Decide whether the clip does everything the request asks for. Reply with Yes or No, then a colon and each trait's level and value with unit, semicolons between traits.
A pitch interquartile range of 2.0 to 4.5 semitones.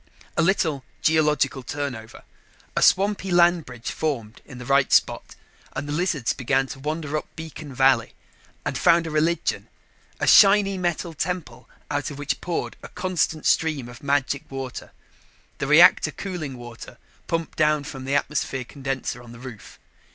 Yes: average, 3.9 semitones